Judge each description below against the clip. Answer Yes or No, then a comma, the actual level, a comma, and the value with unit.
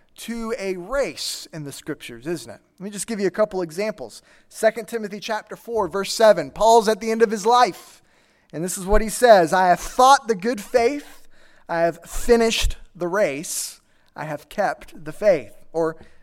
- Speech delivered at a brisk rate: No, average, 190 wpm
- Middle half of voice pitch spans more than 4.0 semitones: Yes, average, 4.6 semitones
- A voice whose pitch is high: Yes, high, 210 Hz